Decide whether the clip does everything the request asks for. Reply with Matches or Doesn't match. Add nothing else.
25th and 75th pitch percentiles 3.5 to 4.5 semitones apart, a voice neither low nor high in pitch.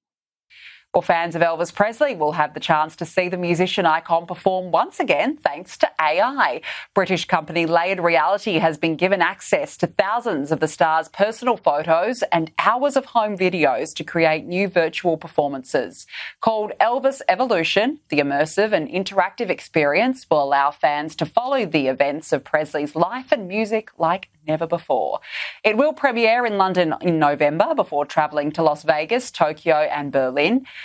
Doesn't match